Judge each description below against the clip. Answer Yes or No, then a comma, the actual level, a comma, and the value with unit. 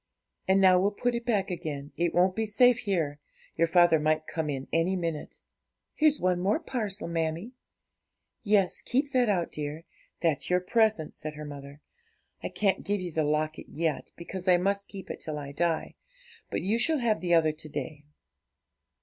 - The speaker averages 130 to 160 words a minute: No, average, 185 wpm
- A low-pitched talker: No, medium, 175 Hz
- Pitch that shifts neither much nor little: Yes, average, 4.7 semitones